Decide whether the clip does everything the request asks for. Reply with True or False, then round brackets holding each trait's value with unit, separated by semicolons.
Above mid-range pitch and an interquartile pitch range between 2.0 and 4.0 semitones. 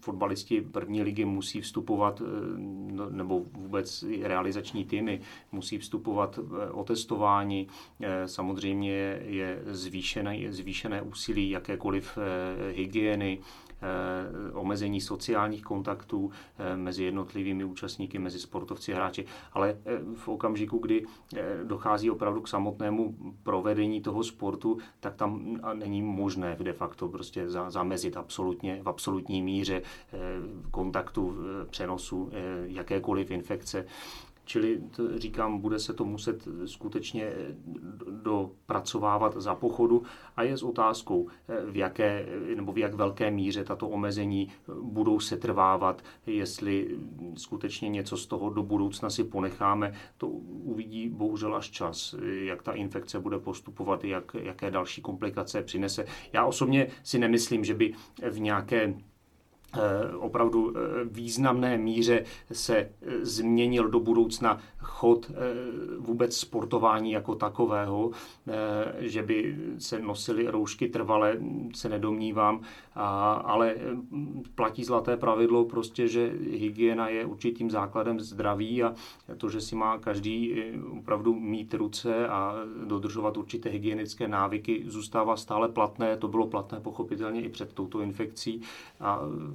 False (105 Hz; 2.7 semitones)